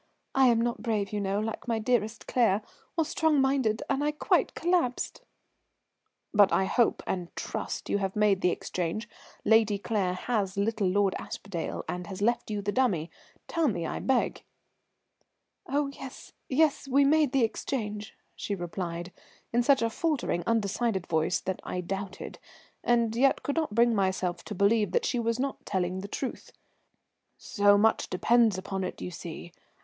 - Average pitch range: Yes, average, 4.4 semitones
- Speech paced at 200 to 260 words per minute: No, average, 165 wpm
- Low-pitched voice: No, high, 215 Hz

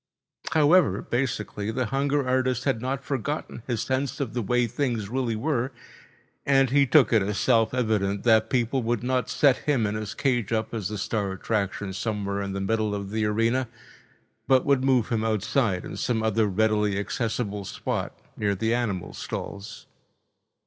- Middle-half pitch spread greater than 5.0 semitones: No, average, 3.7 semitones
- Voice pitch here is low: Yes, low, 115 Hz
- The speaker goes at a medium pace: Yes, average, 170 wpm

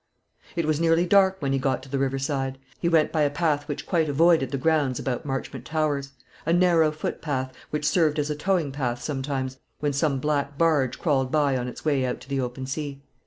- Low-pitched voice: No, medium, 145 Hz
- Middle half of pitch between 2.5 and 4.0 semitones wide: Yes, average, 2.8 semitones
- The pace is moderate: No, fast, 215 wpm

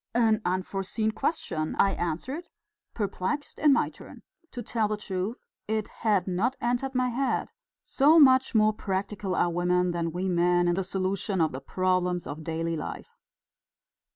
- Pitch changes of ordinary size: Yes, average, 4.6 semitones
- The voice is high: Yes, high, 195 Hz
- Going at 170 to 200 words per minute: No, average, 155 wpm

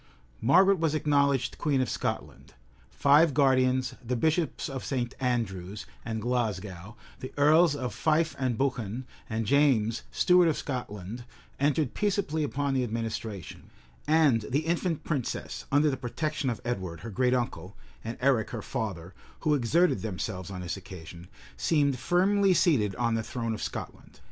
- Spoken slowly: No, average, 150 wpm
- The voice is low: Yes, low, 130 Hz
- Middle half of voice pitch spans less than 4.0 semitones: No, average, 5.1 semitones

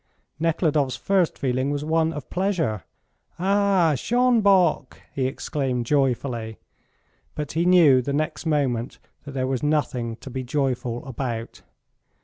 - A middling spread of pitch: Yes, average, 4.3 semitones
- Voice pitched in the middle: Yes, medium, 145 Hz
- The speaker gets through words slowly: Yes, slow, 125 wpm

